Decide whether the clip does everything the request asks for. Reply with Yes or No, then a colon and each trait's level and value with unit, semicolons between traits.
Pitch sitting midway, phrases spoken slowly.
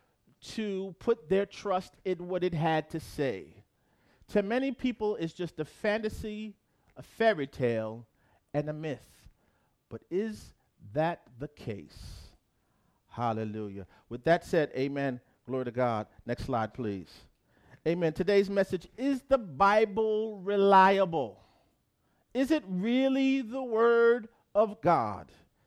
Yes: medium, 170 Hz; slow, 125 wpm